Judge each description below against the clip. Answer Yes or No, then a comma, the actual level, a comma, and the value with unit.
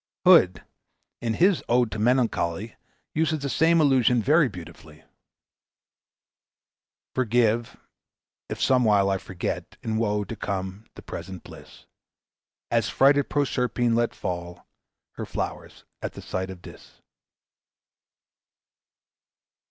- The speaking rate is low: Yes, slow, 110 wpm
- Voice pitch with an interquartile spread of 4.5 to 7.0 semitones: Yes, average, 5.2 semitones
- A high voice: No, low, 115 Hz